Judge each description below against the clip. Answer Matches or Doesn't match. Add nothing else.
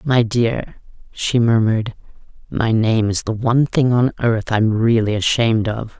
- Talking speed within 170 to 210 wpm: Doesn't match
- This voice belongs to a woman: Matches